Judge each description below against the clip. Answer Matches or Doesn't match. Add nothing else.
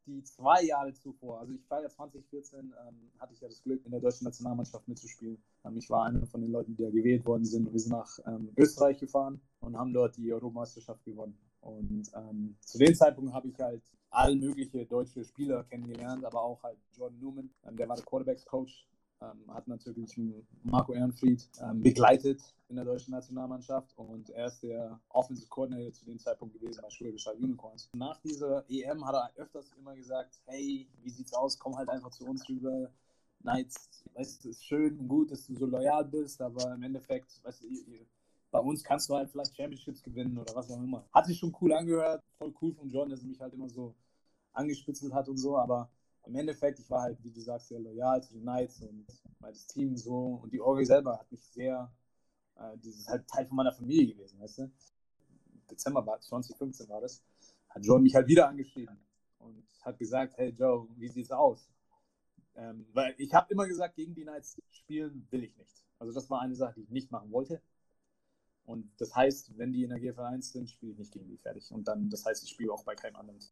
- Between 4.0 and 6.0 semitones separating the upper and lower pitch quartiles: Doesn't match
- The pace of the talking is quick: Matches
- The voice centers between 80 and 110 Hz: Doesn't match